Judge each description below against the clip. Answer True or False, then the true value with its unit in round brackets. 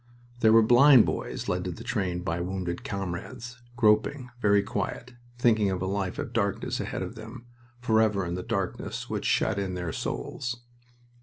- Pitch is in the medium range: False (105 Hz)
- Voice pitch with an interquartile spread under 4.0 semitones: False (4.3 semitones)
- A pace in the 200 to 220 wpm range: False (170 wpm)